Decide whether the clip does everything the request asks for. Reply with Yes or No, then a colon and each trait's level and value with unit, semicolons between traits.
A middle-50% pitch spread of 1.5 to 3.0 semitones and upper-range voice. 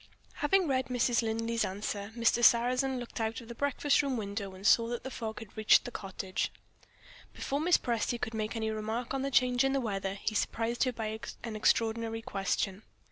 Yes: narrow, 2.5 semitones; high, 230 Hz